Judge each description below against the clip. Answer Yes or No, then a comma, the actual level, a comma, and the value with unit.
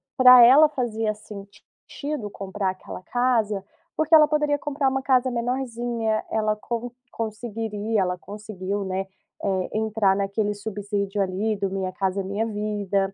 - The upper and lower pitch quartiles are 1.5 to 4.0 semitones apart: Yes, average, 3.4 semitones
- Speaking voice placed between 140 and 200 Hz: No, high, 215 Hz